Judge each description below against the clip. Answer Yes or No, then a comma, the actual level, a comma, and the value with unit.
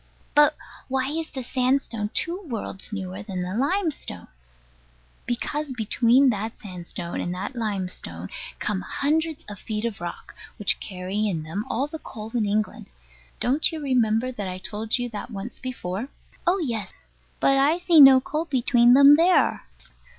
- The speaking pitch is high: Yes, high, 235 Hz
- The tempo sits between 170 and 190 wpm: No, average, 160 wpm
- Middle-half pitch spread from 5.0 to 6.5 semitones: Yes, average, 5.3 semitones